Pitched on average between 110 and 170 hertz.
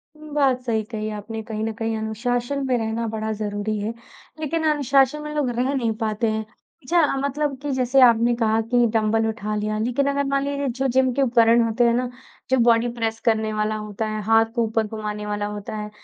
No: high, 230 Hz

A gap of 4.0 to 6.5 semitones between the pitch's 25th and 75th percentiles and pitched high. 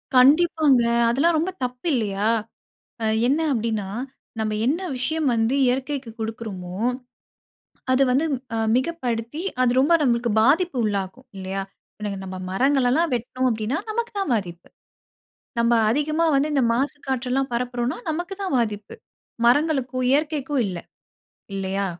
Yes: average, 4.7 semitones; very high, 250 Hz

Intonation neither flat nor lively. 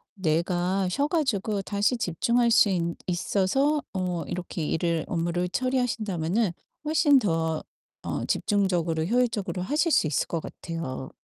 No: wide, 5.8 semitones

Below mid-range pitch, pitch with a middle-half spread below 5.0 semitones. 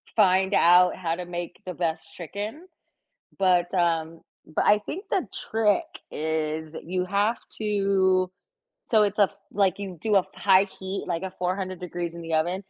No: medium, 185 Hz; average, 2.8 semitones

